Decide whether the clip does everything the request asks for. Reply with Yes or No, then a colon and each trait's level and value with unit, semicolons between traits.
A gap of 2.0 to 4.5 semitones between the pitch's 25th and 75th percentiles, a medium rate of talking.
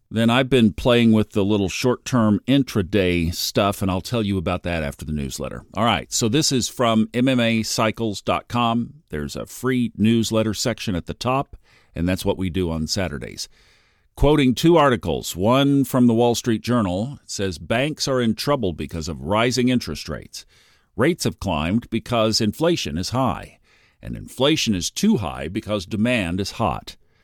No: average, 5.1 semitones; average, 170 wpm